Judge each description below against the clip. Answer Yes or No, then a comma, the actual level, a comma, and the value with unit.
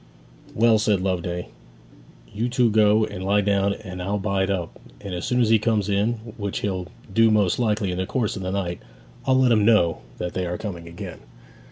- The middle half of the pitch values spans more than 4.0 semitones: No, average, 2.9 semitones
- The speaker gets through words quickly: Yes, fast, 210 wpm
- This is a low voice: Yes, low, 100 Hz